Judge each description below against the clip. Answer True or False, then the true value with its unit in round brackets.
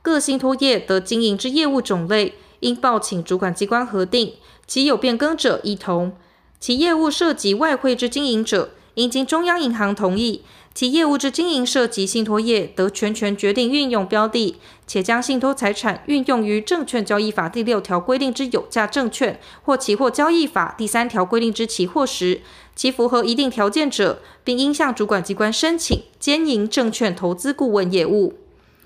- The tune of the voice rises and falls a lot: False (4.9 semitones)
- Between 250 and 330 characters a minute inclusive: True (275 characters per minute)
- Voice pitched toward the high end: True (235 Hz)